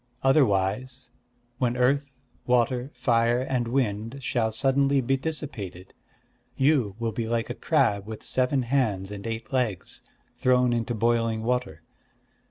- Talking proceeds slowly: Yes, slow, 130 wpm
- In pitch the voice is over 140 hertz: No, low, 120 Hz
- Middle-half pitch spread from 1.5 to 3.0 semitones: Yes, average, 2.7 semitones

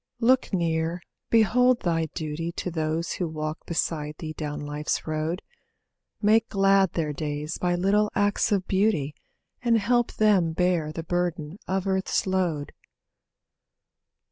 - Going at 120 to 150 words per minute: Yes, slow, 135 wpm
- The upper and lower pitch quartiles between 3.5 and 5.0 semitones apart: Yes, average, 4.0 semitones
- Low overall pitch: No, medium, 175 Hz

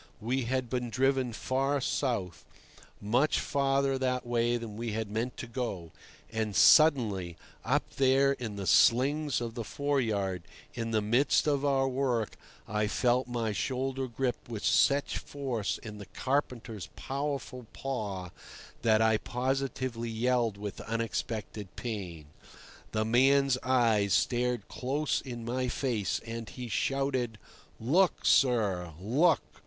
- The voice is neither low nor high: No, low, 120 Hz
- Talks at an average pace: No, slow, 130 wpm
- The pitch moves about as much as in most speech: Yes, average, 3.4 semitones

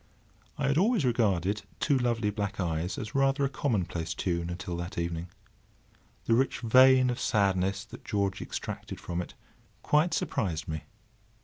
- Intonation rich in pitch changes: Yes, wide, 6.7 semitones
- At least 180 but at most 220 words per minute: No, average, 150 wpm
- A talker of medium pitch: No, low, 105 Hz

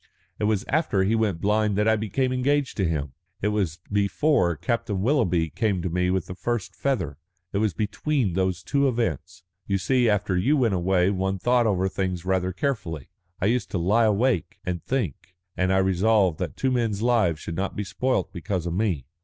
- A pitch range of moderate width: Yes, average, 4.2 semitones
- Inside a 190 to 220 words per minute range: Yes, average, 195 wpm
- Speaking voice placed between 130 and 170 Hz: No, low, 100 Hz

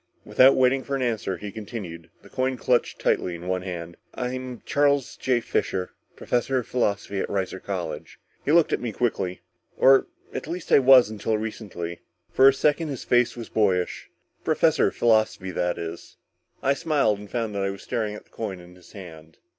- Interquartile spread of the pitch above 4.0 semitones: Yes, wide, 5.6 semitones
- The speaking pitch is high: No, low, 110 Hz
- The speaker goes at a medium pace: Yes, average, 190 wpm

